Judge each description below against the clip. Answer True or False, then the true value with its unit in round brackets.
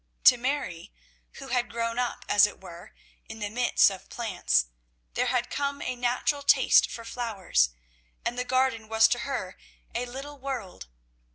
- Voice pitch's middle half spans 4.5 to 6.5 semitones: False (3.6 semitones)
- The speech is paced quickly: False (165 wpm)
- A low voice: False (240 Hz)